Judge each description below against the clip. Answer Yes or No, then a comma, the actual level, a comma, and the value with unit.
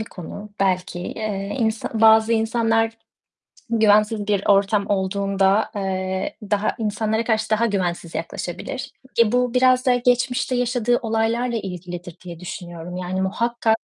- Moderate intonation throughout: Yes, average, 3.2 semitones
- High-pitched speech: Yes, high, 215 Hz